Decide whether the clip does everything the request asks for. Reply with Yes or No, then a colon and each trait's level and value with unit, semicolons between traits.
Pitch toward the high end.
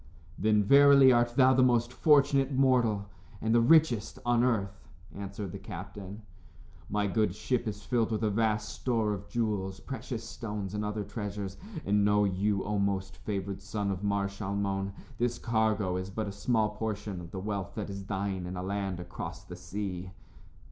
No: low, 105 Hz